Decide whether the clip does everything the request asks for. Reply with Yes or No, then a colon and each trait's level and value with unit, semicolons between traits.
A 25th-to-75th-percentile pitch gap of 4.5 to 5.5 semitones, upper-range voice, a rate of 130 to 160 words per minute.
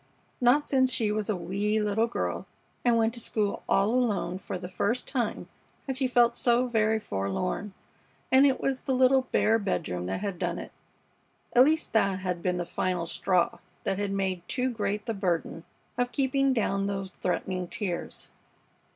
No: average, 4.9 semitones; high, 210 Hz; average, 175 wpm